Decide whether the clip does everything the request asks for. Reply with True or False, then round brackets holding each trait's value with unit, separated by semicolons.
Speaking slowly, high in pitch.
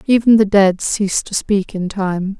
False (200 wpm; 200 Hz)